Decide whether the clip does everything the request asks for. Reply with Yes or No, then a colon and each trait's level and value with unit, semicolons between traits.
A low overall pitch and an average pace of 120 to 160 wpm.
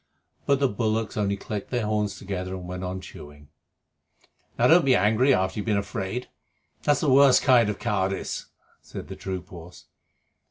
No: low, 105 Hz; average, 170 wpm